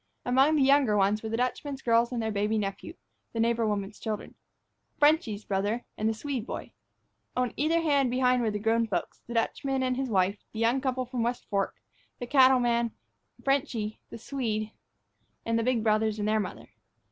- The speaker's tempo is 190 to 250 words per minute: Yes, average, 195 wpm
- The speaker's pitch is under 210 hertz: No, high, 230 Hz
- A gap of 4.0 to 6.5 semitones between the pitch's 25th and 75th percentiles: No, average, 3.2 semitones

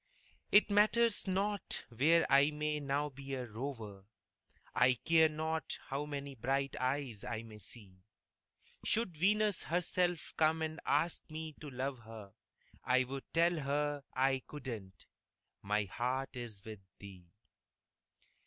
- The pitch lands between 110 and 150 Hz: Yes, medium, 140 Hz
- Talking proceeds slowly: Yes, slow, 130 wpm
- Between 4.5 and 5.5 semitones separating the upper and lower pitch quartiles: Yes, average, 5.1 semitones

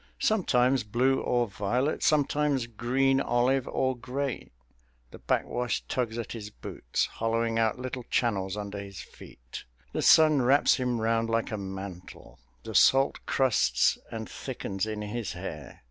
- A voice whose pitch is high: No, low, 120 Hz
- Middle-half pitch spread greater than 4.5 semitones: No, average, 4.0 semitones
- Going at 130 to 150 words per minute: Yes, average, 145 wpm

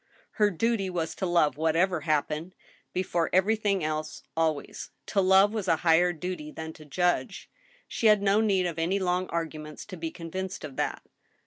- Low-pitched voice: No, medium, 175 Hz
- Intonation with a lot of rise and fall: No, average, 3.0 semitones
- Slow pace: No, average, 175 wpm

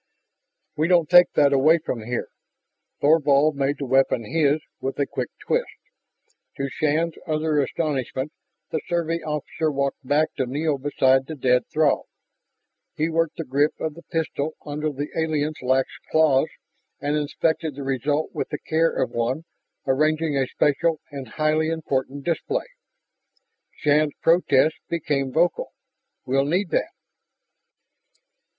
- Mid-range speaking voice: Yes, medium, 150 Hz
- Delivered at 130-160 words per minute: Yes, average, 140 wpm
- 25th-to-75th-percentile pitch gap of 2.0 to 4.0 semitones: Yes, narrow, 2.6 semitones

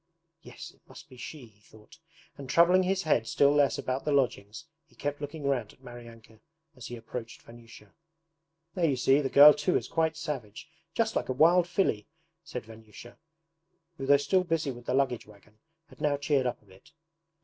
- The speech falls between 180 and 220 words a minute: Yes, average, 195 wpm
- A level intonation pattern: No, average, 4.6 semitones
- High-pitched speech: No, low, 135 Hz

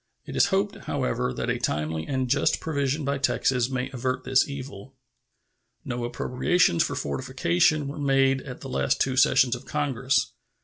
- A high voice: No, low, 130 Hz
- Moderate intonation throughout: No, narrow, 2.1 semitones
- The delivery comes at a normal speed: Yes, average, 165 wpm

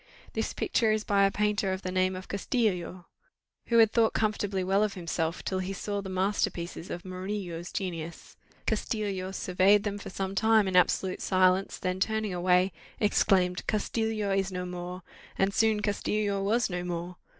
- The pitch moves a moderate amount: No, narrow, 2.3 semitones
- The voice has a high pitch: Yes, high, 195 Hz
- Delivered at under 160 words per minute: No, average, 170 wpm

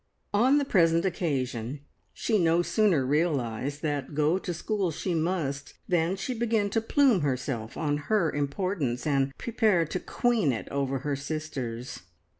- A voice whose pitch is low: No, medium, 160 Hz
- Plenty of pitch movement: Yes, wide, 5.8 semitones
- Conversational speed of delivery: Yes, average, 150 wpm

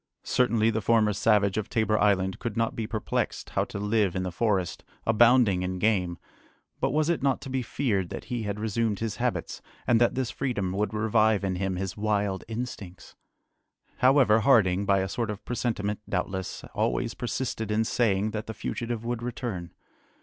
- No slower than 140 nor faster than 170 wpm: No, average, 180 wpm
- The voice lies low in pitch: Yes, low, 110 Hz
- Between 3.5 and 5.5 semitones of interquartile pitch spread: No, average, 3.1 semitones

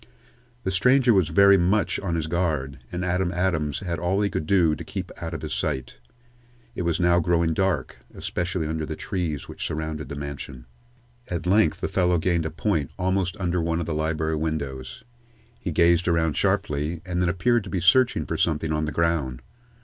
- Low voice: Yes, very low, 85 Hz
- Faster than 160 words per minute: Yes, average, 195 wpm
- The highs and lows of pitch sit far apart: No, average, 2.9 semitones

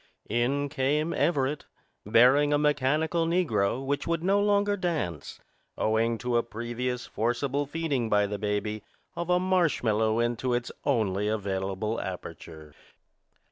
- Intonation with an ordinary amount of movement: No, wide, 5.7 semitones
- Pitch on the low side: Yes, low, 125 Hz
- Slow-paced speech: Yes, slow, 130 wpm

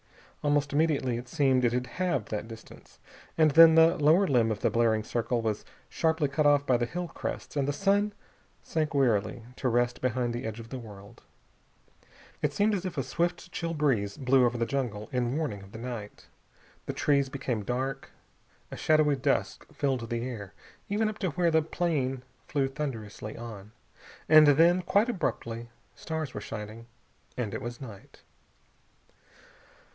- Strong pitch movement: No, average, 5.0 semitones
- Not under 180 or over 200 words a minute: No, average, 170 wpm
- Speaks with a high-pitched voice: No, low, 130 Hz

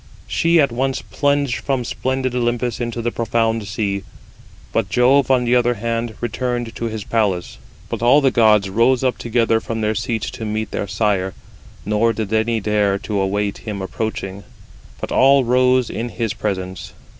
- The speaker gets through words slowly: No, average, 175 wpm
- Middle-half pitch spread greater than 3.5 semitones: No, average, 2.7 semitones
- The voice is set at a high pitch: No, low, 115 Hz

